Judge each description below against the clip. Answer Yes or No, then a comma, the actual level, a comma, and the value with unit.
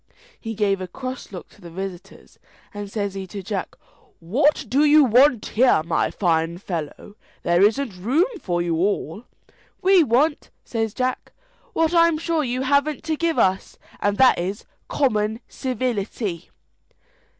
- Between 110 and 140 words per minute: No, average, 150 wpm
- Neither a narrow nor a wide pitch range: No, wide, 6.4 semitones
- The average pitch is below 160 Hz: No, high, 215 Hz